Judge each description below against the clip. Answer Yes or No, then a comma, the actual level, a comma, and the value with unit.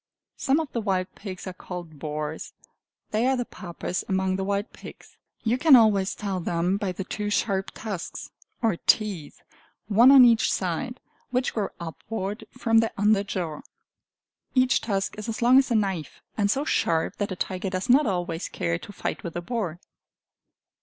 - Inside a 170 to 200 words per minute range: Yes, average, 180 wpm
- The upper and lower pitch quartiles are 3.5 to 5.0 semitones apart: Yes, average, 3.9 semitones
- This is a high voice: Yes, high, 200 Hz